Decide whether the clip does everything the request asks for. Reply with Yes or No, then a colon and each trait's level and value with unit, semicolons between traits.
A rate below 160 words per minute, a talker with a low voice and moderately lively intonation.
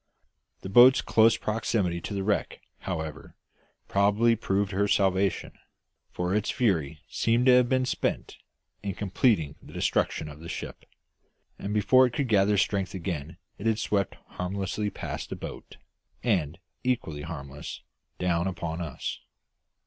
Yes: average, 140 wpm; low, 100 Hz; average, 4.5 semitones